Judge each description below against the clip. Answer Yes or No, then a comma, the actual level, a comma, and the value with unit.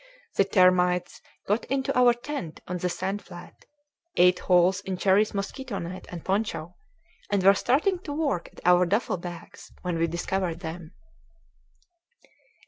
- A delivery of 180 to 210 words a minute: No, average, 145 wpm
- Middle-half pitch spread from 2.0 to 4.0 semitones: Yes, average, 2.9 semitones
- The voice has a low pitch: No, medium, 185 Hz